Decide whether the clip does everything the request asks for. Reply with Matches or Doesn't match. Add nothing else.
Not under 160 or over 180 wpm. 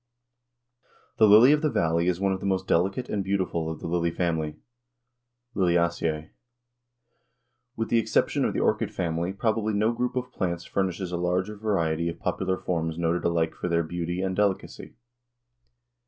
Matches